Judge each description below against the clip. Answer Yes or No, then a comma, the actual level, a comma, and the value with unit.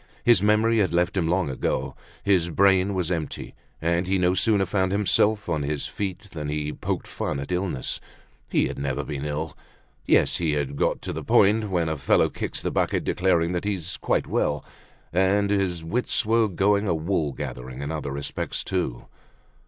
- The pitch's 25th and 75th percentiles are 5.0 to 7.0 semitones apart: No, average, 4.3 semitones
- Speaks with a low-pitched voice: Yes, very low, 90 Hz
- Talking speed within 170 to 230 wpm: Yes, average, 185 wpm